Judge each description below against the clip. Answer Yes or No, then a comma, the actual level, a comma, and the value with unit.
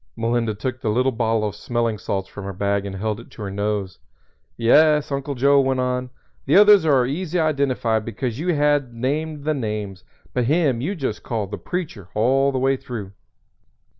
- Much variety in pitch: No, average, 4.8 semitones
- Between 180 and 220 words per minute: Yes, average, 190 wpm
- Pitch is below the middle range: Yes, low, 125 Hz